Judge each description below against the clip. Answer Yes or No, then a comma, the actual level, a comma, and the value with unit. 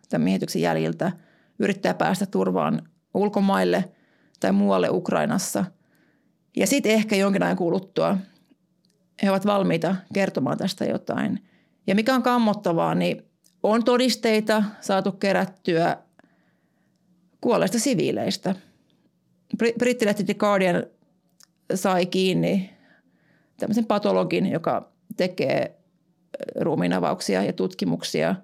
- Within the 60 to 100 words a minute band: Yes, slow, 95 wpm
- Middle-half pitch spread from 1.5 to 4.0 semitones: Yes, average, 2.9 semitones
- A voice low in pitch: No, high, 195 Hz